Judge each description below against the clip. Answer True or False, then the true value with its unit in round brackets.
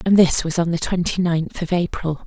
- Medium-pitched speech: True (170 Hz)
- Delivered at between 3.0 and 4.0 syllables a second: False (5.1 syllables/s)